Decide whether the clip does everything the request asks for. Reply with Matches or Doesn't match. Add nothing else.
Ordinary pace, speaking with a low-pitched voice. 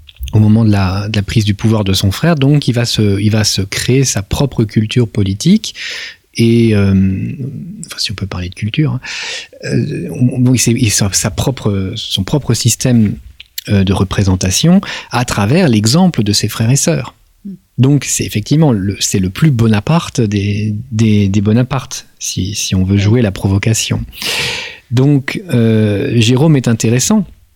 Matches